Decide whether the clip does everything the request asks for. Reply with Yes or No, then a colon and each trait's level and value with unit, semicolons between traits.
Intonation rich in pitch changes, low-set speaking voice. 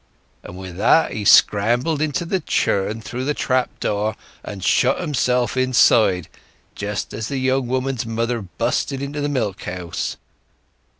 No: average, 4.5 semitones; low, 120 Hz